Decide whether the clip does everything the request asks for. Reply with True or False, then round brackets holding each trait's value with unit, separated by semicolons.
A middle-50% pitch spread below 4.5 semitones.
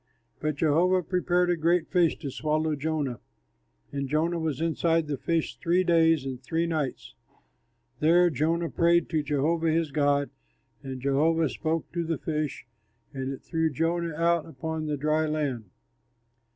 True (2.5 semitones)